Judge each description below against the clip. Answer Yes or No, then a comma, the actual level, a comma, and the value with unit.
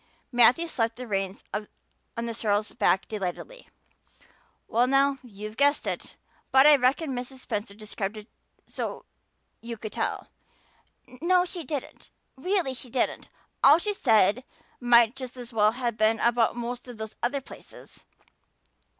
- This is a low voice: No, high, 240 Hz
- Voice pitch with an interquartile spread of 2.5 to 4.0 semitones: Yes, average, 3.6 semitones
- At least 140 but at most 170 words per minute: Yes, average, 145 wpm